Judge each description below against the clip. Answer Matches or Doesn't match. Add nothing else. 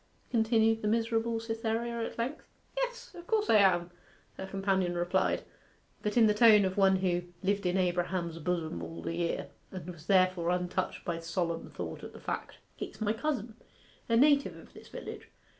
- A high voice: Matches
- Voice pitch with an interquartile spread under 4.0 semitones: Doesn't match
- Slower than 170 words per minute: Doesn't match